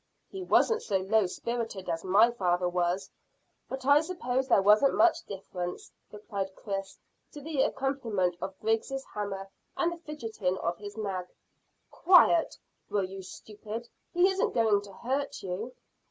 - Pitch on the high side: Yes, high, 210 Hz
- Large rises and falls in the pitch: Yes, wide, 5.8 semitones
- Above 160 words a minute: No, average, 150 wpm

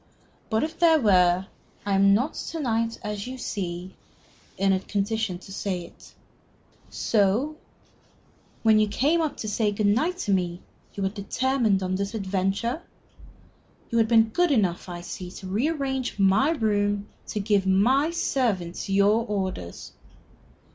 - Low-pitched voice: No, high, 205 Hz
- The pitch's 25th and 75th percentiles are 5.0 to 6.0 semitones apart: No, average, 4.3 semitones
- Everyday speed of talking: Yes, average, 150 wpm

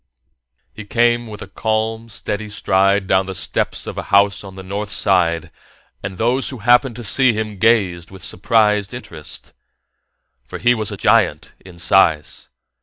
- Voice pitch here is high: No, low, 100 Hz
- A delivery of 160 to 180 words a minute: Yes, average, 165 wpm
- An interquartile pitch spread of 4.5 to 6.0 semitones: No, average, 2.9 semitones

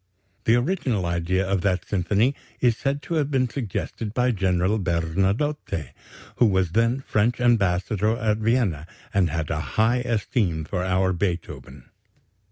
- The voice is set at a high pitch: No, low, 100 Hz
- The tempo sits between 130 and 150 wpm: Yes, average, 145 wpm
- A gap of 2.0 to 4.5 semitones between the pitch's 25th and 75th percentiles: No, average, 5.2 semitones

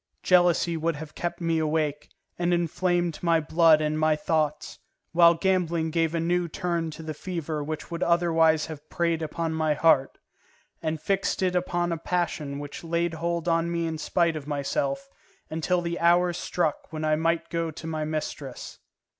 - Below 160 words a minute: No, average, 175 wpm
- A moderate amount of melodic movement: No, narrow, 1.8 semitones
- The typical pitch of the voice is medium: Yes, medium, 165 Hz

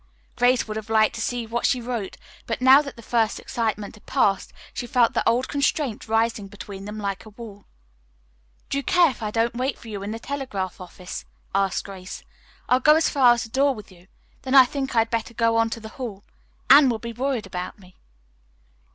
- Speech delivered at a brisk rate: Yes, fast, 220 wpm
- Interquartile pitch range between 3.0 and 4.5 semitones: Yes, average, 3.5 semitones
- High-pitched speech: Yes, high, 230 Hz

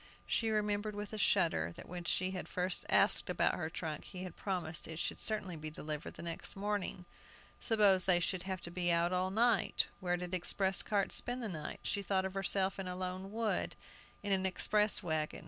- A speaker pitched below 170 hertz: No, medium, 185 Hz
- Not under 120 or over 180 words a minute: No, fast, 205 wpm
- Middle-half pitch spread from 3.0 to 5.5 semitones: No, narrow, 2.6 semitones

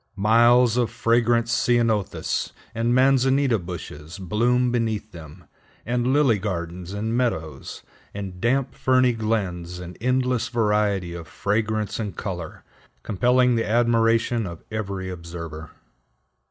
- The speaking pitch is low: Yes, low, 110 Hz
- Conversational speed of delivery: No, slow, 115 wpm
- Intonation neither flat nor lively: Yes, average, 4.7 semitones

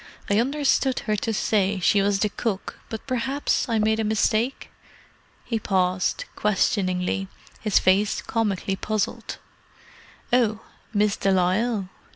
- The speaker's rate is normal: No, slow, 125 wpm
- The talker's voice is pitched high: Yes, high, 210 Hz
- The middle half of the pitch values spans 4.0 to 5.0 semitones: No, average, 2.7 semitones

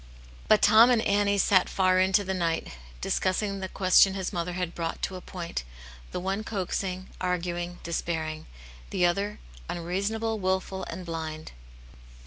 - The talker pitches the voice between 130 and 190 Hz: Yes, medium, 185 Hz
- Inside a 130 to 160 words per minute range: Yes, average, 150 wpm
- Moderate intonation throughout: No, narrow, 2.3 semitones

